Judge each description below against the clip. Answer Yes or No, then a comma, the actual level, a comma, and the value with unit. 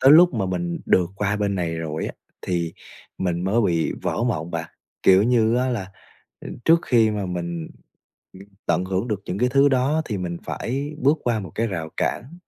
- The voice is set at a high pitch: No, low, 100 Hz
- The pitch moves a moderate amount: No, wide, 5.9 semitones